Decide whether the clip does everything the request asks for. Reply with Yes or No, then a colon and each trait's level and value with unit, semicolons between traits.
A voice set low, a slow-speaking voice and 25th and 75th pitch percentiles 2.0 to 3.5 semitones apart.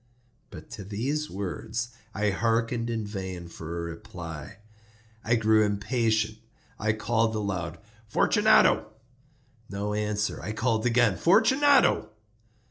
Yes: low, 110 Hz; slow, 115 wpm; average, 2.7 semitones